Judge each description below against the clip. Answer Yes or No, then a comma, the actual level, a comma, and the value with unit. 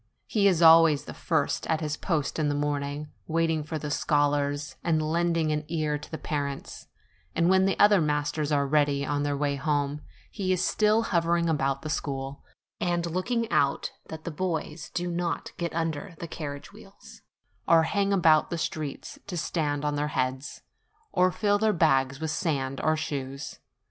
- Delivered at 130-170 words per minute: No, average, 180 wpm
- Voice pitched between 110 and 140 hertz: No, medium, 155 Hz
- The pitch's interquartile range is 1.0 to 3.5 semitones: Yes, average, 2.8 semitones